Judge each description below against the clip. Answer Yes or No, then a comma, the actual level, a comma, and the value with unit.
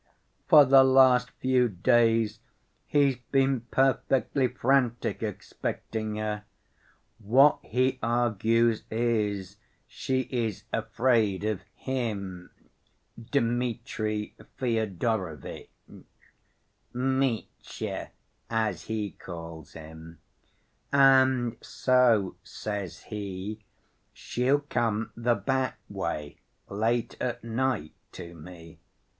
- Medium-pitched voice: No, low, 115 Hz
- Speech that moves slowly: Yes, slow, 80 wpm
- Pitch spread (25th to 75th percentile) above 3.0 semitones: Yes, average, 3.9 semitones